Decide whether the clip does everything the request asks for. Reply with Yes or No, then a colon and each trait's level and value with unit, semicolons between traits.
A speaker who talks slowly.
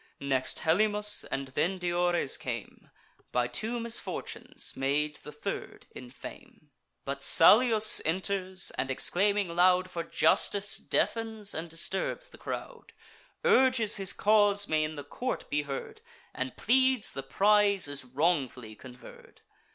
Yes: slow, 130 wpm